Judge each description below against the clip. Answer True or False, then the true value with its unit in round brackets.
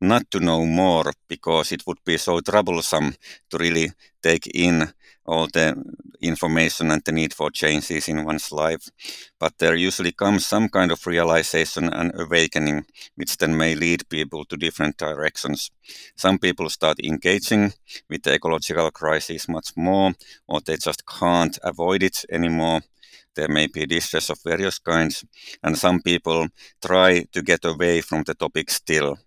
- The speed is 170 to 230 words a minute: False (160 wpm)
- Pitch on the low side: True (80 Hz)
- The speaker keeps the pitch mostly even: True (1.7 semitones)